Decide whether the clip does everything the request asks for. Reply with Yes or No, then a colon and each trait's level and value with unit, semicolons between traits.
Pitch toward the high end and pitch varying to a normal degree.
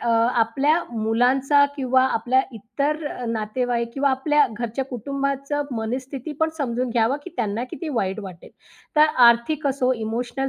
Yes: very high, 255 Hz; average, 3.2 semitones